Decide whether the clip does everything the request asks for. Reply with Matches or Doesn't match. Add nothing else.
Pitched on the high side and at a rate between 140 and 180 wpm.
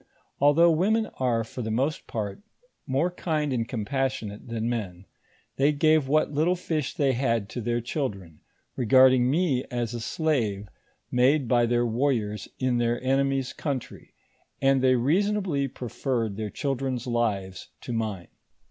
Doesn't match